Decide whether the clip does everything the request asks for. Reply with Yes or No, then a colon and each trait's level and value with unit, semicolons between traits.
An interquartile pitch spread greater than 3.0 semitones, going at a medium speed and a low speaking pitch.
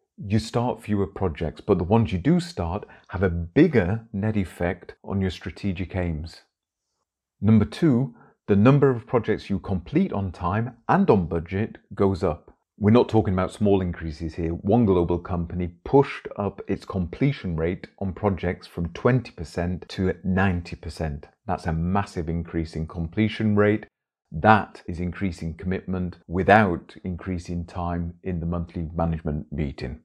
Yes: average, 3.5 semitones; average, 150 wpm; very low, 95 Hz